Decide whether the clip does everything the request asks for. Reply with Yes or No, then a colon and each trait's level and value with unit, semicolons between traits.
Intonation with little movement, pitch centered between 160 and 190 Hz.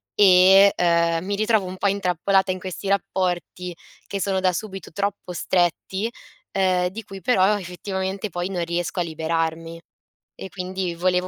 Yes: narrow, 1.8 semitones; medium, 185 Hz